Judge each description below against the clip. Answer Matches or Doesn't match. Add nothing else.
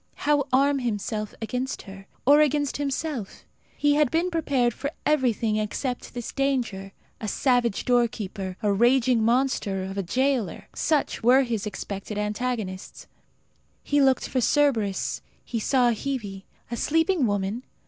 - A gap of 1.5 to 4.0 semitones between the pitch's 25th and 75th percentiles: Doesn't match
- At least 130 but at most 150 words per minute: Matches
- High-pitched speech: Matches